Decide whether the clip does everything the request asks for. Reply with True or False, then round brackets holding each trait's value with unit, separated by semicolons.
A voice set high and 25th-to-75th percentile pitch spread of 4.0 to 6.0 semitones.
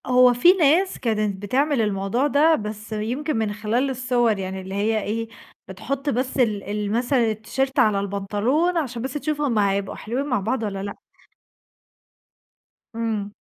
True (230 Hz; 4.4 semitones)